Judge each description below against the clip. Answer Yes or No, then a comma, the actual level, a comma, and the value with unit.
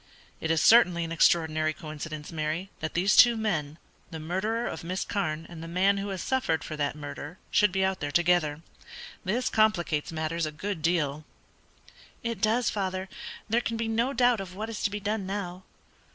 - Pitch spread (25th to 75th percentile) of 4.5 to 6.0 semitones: Yes, average, 5.0 semitones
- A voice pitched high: No, medium, 180 Hz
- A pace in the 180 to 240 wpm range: Yes, average, 190 wpm